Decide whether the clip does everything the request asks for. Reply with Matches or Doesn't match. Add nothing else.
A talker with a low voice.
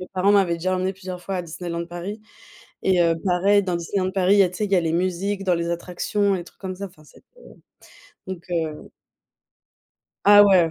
Doesn't match